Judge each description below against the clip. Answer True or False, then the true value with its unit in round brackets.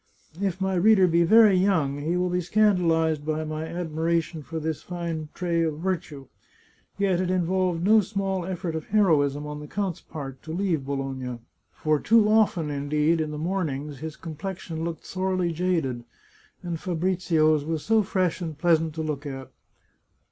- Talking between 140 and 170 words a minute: True (165 wpm)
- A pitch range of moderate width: True (3.3 semitones)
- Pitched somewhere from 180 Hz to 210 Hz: False (165 Hz)